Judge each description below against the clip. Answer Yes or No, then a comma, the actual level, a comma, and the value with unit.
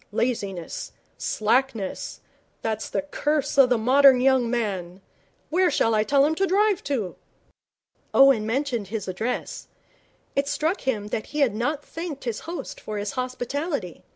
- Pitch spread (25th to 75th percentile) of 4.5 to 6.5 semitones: Yes, average, 4.9 semitones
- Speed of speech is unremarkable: Yes, average, 150 wpm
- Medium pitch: No, very high, 255 Hz